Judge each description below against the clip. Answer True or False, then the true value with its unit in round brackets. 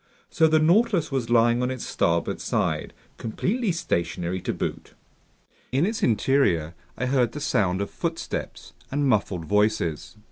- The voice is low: True (120 Hz)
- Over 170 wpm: False (145 wpm)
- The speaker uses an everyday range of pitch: False (8.0 semitones)